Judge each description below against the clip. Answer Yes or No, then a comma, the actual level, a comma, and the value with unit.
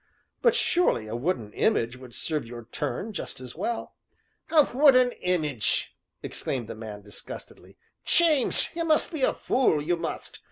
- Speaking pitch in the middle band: Yes, medium, 155 Hz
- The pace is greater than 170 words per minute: No, average, 155 wpm